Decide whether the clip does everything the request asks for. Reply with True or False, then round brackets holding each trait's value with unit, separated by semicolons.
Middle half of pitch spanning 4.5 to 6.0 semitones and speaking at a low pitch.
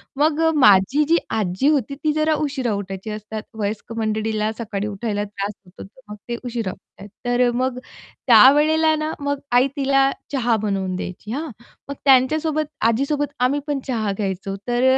False (5.2 semitones; 240 Hz)